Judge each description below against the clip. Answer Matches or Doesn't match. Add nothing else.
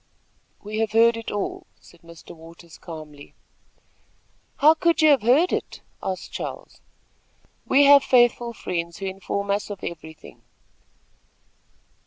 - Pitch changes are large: Matches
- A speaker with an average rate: Doesn't match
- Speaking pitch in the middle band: Doesn't match